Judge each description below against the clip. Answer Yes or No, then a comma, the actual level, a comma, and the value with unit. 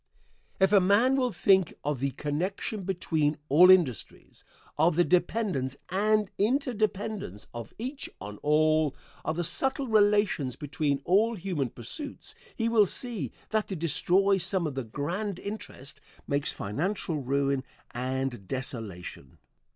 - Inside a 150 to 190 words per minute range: No, slow, 135 wpm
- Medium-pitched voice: Yes, medium, 175 Hz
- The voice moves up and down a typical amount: No, wide, 6.9 semitones